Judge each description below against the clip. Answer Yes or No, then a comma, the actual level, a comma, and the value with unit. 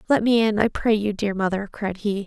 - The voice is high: Yes, high, 205 Hz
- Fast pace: Yes, fast, 265 wpm